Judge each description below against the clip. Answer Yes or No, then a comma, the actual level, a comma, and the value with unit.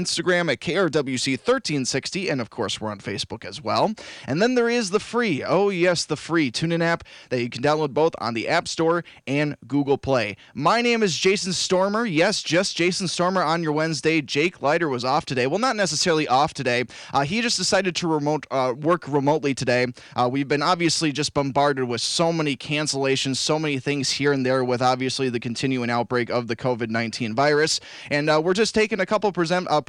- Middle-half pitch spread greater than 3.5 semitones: Yes, average, 5.1 semitones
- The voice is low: No, medium, 150 Hz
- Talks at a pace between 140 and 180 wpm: No, fast, 205 wpm